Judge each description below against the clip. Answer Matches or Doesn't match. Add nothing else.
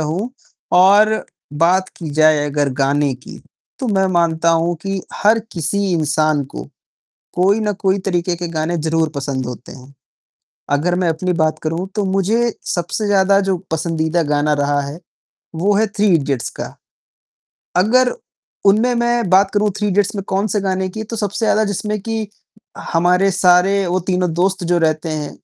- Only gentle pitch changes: Doesn't match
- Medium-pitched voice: Matches